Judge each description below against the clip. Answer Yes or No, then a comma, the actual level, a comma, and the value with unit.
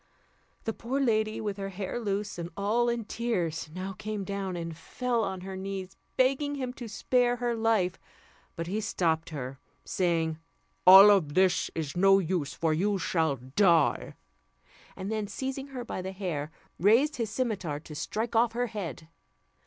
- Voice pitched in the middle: No, high, 195 Hz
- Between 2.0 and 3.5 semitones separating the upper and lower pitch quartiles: No, average, 4.9 semitones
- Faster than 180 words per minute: No, average, 170 wpm